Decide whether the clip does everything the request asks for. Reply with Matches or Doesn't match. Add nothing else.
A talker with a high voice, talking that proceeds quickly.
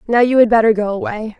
Matches